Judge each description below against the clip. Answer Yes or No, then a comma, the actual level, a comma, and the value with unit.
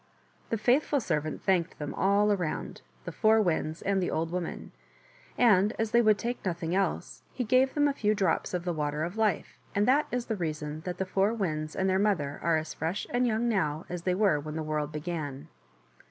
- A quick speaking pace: Yes, fast, 220 wpm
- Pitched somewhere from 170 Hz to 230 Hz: Yes, medium, 185 Hz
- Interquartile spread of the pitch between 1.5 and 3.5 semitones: No, wide, 5.4 semitones